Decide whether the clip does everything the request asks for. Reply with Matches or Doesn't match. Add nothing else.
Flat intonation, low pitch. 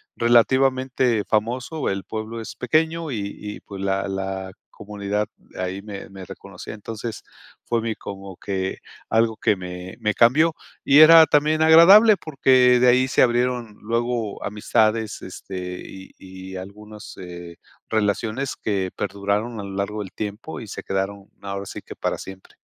Doesn't match